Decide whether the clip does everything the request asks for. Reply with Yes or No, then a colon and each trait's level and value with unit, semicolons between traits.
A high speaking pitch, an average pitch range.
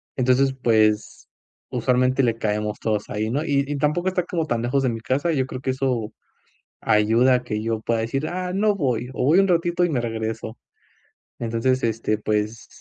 No: low, 125 Hz; average, 4.0 semitones